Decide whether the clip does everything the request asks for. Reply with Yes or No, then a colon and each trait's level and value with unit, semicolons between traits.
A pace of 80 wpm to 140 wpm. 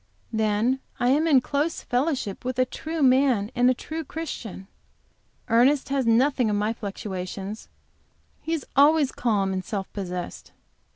No: average, 150 wpm